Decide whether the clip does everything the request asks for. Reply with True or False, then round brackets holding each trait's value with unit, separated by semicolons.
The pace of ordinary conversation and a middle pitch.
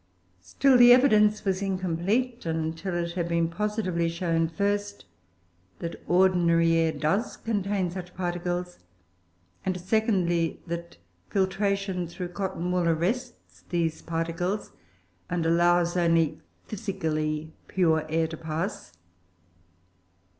False (110 wpm; 175 Hz)